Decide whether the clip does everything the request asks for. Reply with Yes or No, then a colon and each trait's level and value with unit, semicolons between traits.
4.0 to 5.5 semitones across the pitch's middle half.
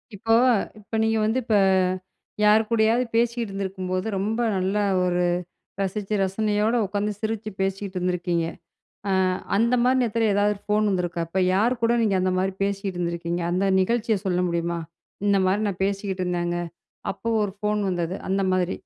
No: average, 2.9 semitones